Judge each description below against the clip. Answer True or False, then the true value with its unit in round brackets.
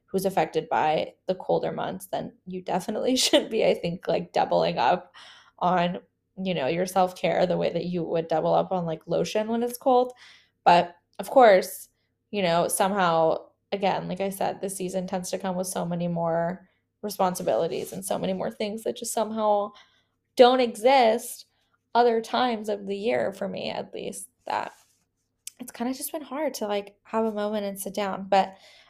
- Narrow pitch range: False (4.2 semitones)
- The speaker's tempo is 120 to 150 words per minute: False (185 wpm)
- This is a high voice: True (200 Hz)